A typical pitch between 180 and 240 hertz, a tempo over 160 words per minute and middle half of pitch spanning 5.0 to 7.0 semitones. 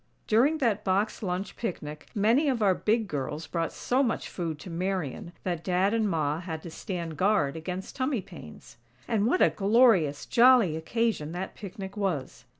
Yes: high, 190 Hz; average, 170 wpm; average, 5.3 semitones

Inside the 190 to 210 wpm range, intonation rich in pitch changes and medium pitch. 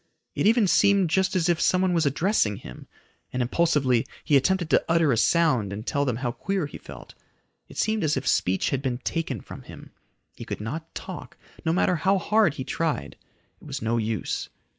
Yes: average, 200 wpm; wide, 6.6 semitones; medium, 155 Hz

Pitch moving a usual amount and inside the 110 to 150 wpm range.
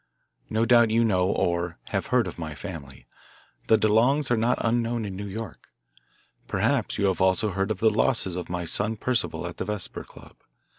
No: average, 3.7 semitones; average, 190 wpm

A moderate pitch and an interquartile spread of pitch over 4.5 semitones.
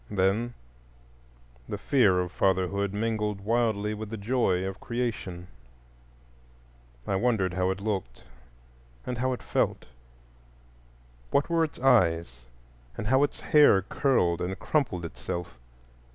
No: very low, 95 Hz; wide, 5.4 semitones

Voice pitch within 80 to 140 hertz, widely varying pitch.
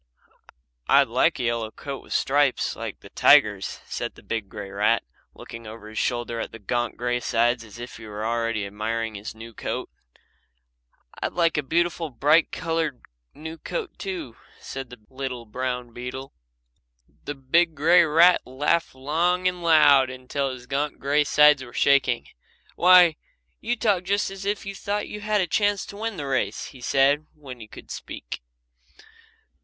Yes: low, 135 Hz; wide, 6.1 semitones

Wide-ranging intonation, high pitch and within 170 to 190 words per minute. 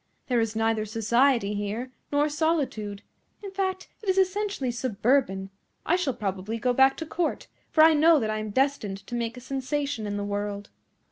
Yes: wide, 5.9 semitones; high, 245 Hz; average, 185 wpm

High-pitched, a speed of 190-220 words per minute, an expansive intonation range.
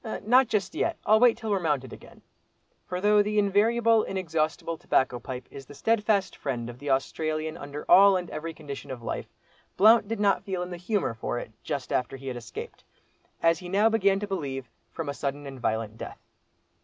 No: medium, 165 Hz; average, 200 wpm; wide, 7.1 semitones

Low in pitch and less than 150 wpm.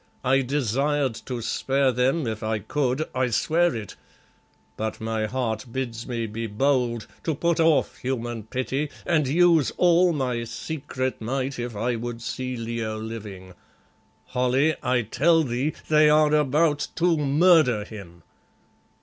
Yes: low, 130 Hz; average, 140 wpm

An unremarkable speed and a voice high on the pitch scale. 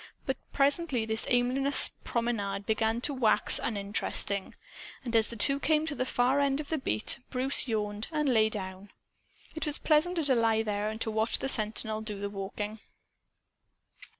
Yes: average, 170 wpm; high, 230 Hz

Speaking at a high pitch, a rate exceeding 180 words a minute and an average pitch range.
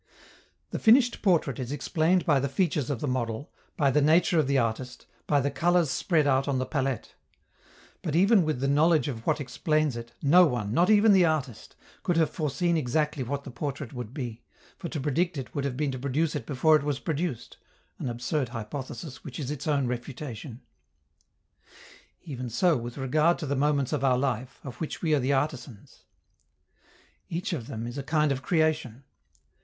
No: medium, 140 Hz; average, 190 wpm; average, 3.6 semitones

